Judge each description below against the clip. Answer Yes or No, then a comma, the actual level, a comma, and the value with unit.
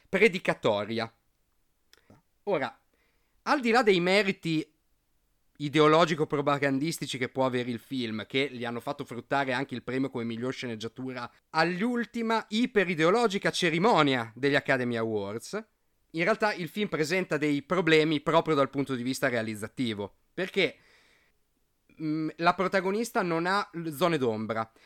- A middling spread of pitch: No, wide, 6.5 semitones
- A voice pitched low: No, medium, 150 Hz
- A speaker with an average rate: Yes, average, 125 wpm